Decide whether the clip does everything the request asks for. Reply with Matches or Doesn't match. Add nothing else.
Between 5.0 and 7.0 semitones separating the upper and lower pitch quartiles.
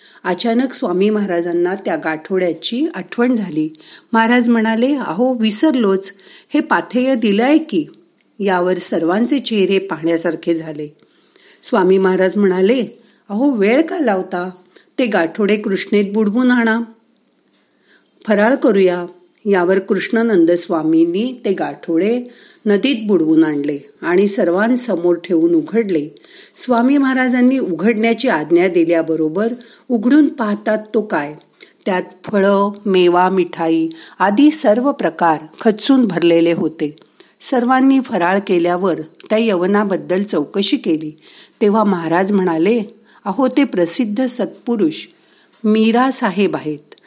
Matches